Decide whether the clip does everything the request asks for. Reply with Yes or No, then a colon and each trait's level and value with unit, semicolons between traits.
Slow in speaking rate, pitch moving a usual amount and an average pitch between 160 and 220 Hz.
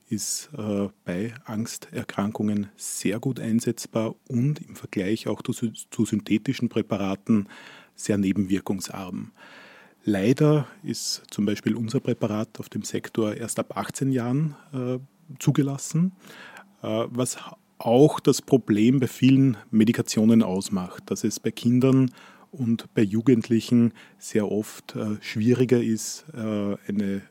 No: slow, 110 wpm; average, 3.5 semitones; low, 115 Hz